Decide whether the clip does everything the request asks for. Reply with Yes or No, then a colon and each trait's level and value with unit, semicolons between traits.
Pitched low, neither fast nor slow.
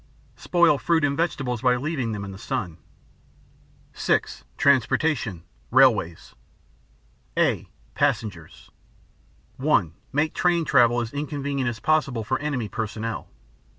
No: low, 130 Hz; slow, 115 wpm